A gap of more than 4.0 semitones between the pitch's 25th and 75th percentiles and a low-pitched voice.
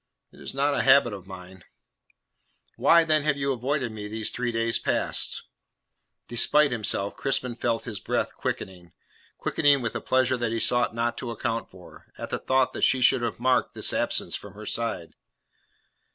No: average, 3.4 semitones; low, 120 Hz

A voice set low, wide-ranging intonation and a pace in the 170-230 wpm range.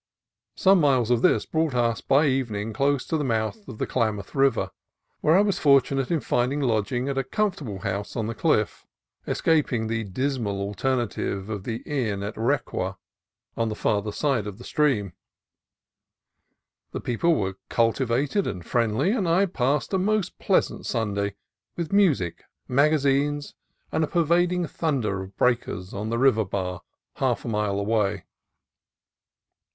No: low, 125 Hz; wide, 5.8 semitones; average, 155 wpm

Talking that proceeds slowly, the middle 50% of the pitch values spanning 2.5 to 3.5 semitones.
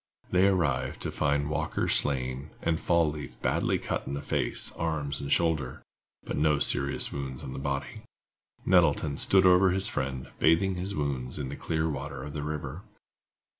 No: average, 170 wpm; average, 3.1 semitones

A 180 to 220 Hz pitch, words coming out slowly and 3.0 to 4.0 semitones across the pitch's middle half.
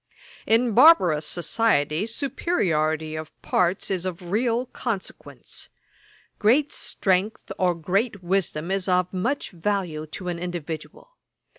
No: medium, 185 Hz; slow, 115 wpm; average, 5.1 semitones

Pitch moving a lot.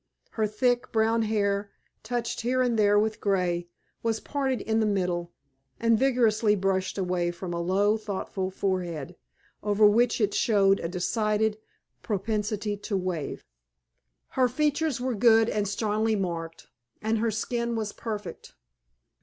No: average, 2.9 semitones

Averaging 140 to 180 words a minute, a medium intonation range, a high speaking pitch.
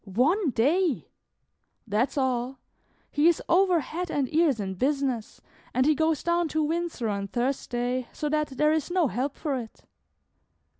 Yes: average, 155 wpm; average, 4.7 semitones; very high, 280 Hz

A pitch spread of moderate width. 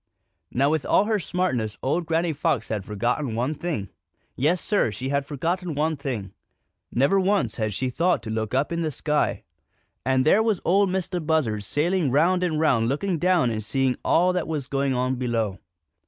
No: wide, 6.0 semitones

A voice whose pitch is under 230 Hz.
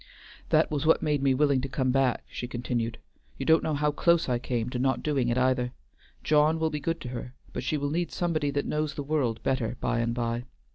Yes: low, 135 Hz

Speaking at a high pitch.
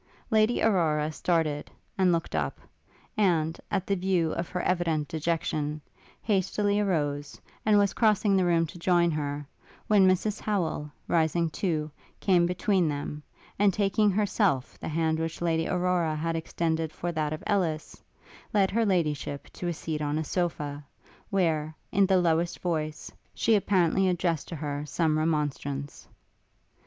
No: medium, 170 Hz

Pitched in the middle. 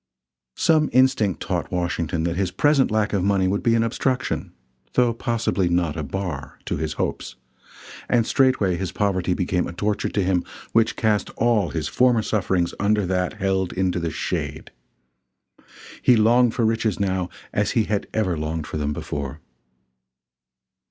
No: very low, 95 Hz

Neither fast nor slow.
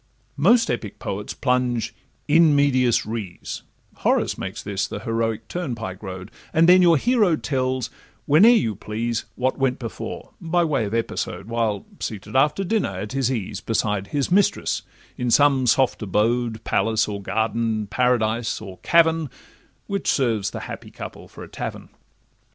Yes: average, 150 wpm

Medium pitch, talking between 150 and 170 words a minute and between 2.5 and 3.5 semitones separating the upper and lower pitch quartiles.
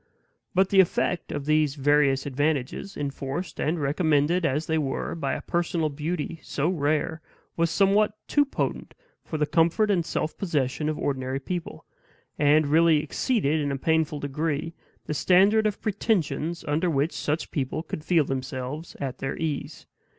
Yes: medium, 155 Hz; average, 160 wpm; average, 3.2 semitones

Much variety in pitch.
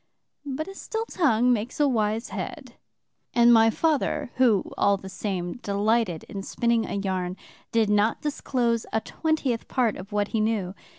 No: average, 3.7 semitones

